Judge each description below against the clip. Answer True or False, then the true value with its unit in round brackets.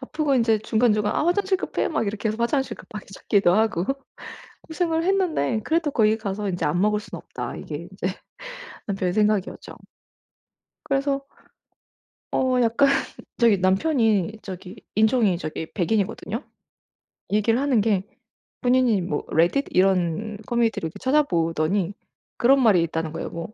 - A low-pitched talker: False (215 Hz)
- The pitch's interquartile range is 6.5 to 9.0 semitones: False (5.5 semitones)